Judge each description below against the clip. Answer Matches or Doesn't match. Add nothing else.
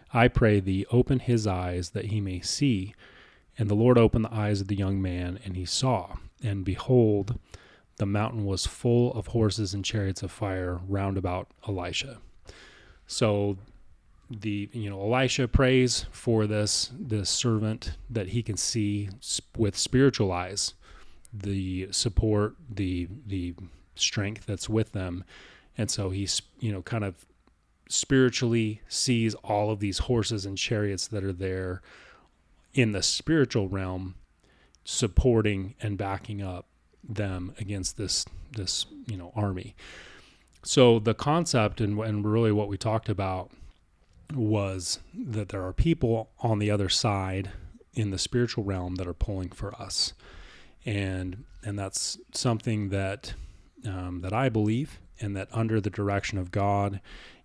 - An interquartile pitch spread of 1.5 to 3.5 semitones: Matches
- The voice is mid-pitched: Doesn't match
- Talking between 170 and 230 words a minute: Doesn't match